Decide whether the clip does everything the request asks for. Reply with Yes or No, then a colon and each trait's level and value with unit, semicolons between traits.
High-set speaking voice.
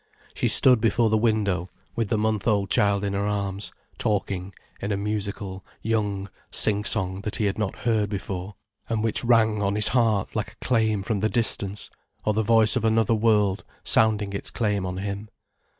No: low, 105 Hz